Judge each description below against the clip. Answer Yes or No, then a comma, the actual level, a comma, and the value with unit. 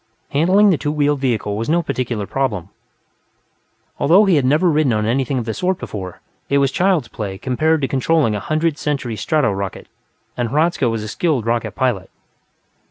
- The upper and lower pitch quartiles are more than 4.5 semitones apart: Yes, wide, 5.6 semitones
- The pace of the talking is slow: No, average, 180 wpm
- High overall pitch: No, low, 135 Hz